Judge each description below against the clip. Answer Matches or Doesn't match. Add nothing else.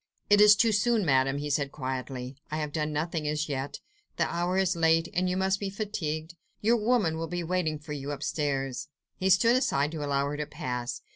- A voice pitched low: Doesn't match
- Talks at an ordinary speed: Doesn't match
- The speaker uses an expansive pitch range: Doesn't match